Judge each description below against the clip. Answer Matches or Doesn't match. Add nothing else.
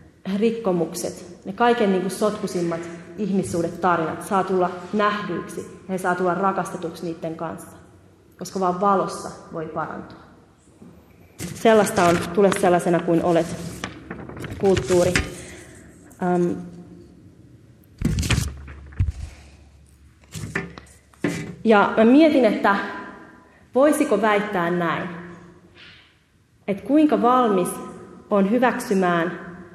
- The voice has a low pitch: Doesn't match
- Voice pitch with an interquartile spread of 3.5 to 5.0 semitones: Doesn't match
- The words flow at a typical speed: Doesn't match